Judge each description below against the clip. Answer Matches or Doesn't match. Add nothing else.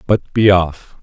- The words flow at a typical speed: Matches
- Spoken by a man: Matches